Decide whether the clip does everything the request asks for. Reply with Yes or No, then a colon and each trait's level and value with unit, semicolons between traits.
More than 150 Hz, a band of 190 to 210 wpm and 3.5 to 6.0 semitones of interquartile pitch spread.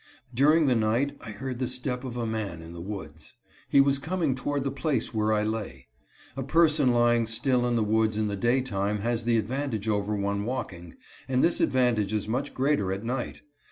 No: low, 120 Hz; fast, 205 wpm; average, 3.9 semitones